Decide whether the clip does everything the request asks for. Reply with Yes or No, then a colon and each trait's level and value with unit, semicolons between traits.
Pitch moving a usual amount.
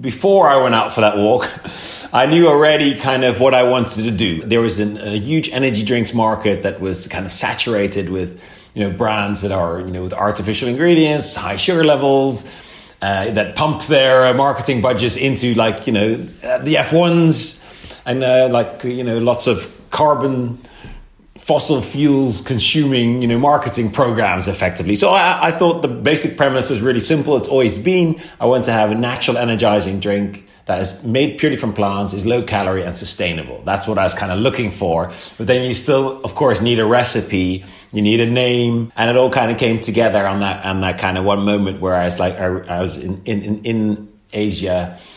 Yes: average, 4.7 semitones